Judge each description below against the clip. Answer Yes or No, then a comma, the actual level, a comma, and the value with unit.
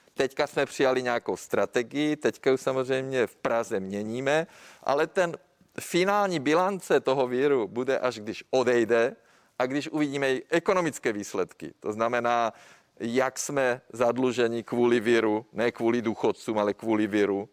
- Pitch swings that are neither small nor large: Yes, average, 3.3 semitones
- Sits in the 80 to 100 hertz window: No, low, 125 Hz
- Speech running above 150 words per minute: No, average, 135 wpm